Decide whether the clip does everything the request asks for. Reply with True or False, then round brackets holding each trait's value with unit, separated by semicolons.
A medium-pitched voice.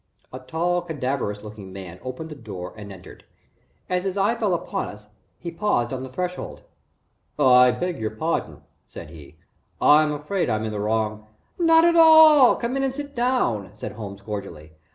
False (130 Hz)